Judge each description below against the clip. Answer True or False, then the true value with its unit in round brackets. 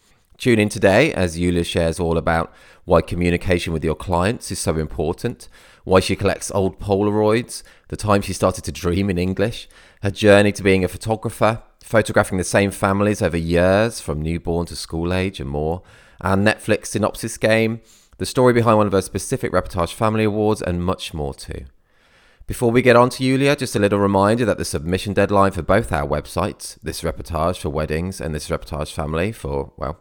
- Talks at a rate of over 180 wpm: True (190 wpm)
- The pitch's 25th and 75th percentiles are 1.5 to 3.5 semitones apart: False (4.2 semitones)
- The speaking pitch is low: True (95 Hz)